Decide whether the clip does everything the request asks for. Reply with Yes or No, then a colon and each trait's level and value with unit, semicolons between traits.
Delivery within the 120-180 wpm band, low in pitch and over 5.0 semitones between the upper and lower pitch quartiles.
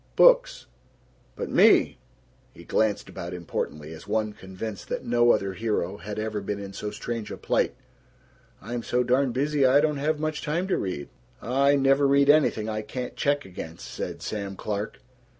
Yes: average, 170 wpm; low, 115 Hz; wide, 5.6 semitones